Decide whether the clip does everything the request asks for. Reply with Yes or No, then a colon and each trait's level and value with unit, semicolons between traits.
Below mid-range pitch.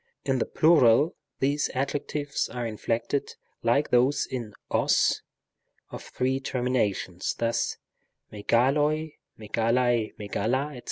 Yes: low, 125 Hz